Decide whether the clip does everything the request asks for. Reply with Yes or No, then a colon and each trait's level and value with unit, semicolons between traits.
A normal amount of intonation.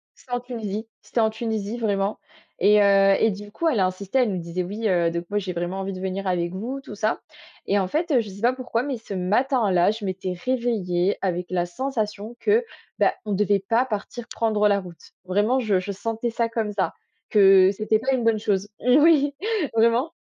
Yes: average, 3.6 semitones